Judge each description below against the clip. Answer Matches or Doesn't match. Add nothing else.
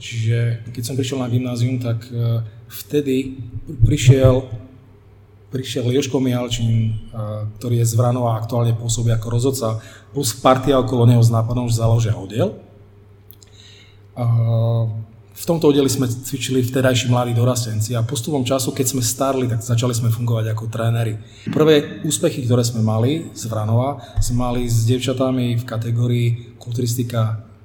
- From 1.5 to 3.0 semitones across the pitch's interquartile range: Matches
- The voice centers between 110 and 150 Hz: Matches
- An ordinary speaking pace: Matches